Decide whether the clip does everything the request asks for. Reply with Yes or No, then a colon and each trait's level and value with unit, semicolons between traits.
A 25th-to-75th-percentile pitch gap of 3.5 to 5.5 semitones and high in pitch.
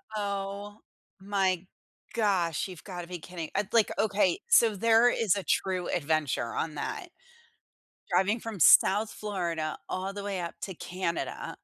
No: average, 2.9 semitones; high, 195 Hz